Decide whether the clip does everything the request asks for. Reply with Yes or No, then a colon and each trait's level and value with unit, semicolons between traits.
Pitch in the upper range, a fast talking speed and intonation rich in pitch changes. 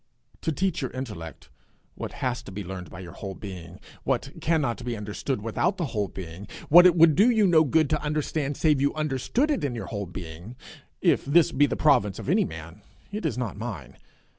No: low, 125 Hz; fast, 210 wpm; wide, 8.0 semitones